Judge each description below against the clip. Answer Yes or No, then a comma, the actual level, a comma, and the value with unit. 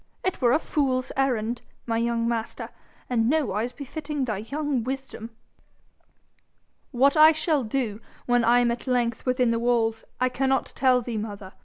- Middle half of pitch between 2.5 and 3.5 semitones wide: Yes, average, 2.8 semitones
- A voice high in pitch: Yes, high, 245 Hz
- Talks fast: No, average, 155 wpm